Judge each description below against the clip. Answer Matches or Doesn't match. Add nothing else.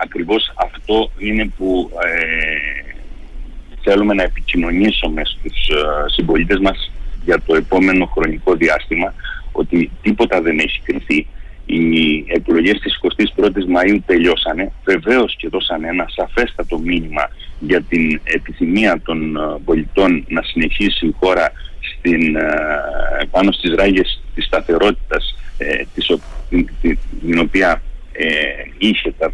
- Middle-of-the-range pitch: Doesn't match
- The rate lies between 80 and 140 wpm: Matches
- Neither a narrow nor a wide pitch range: Matches